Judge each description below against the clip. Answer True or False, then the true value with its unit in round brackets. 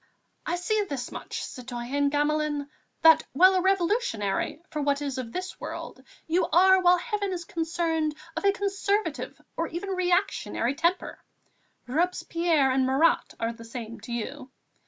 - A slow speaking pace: False (155 wpm)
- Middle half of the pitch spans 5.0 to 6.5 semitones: True (5.5 semitones)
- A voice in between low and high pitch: False (320 Hz)